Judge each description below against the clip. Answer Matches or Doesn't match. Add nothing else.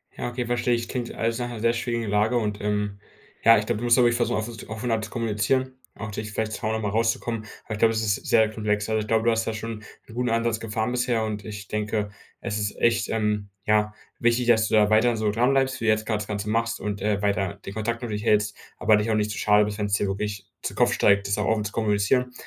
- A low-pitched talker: Matches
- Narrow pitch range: Matches